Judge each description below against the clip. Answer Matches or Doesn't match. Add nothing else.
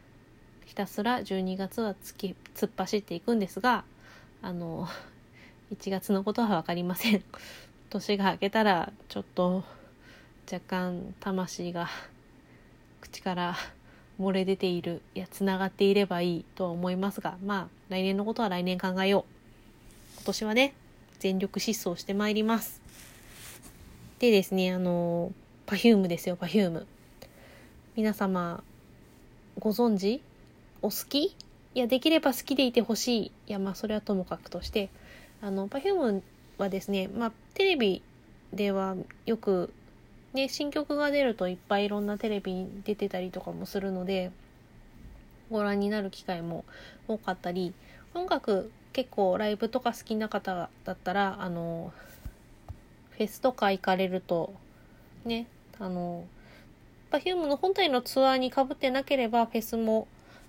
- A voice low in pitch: Doesn't match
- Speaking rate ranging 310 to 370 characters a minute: Doesn't match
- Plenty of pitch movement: Doesn't match